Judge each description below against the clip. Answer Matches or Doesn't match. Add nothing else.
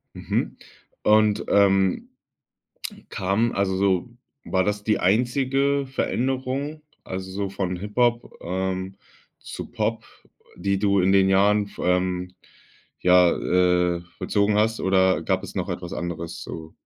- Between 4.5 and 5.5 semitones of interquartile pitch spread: Doesn't match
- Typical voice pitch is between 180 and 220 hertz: Doesn't match